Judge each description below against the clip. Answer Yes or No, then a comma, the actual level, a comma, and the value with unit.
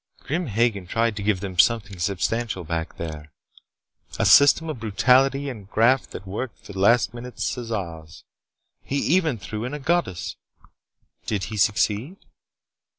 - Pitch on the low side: Yes, low, 110 Hz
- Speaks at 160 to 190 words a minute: No, average, 150 wpm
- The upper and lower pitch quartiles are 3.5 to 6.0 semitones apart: Yes, average, 5.1 semitones